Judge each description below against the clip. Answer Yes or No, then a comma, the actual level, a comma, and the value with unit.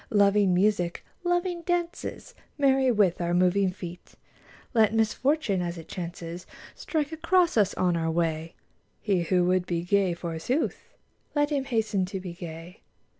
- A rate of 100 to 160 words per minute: Yes, average, 145 wpm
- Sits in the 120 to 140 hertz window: No, high, 195 Hz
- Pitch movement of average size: No, wide, 6.9 semitones